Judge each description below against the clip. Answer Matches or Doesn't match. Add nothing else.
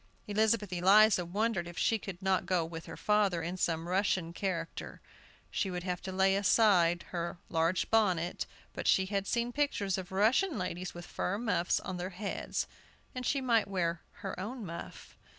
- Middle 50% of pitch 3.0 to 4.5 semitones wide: Matches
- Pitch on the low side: Doesn't match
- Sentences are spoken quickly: Doesn't match